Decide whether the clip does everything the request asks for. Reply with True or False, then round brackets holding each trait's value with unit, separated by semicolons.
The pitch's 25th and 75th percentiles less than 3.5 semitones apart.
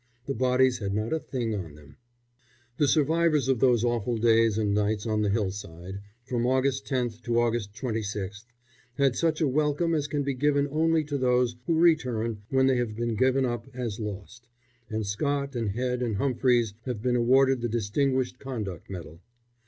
False (3.9 semitones)